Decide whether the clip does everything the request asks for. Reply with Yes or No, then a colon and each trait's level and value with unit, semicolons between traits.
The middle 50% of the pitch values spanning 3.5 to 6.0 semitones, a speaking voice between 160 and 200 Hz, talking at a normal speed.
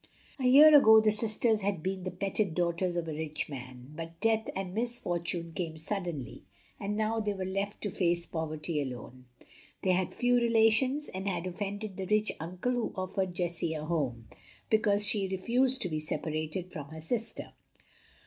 Yes: average, 4.8 semitones; medium, 185 Hz; average, 175 wpm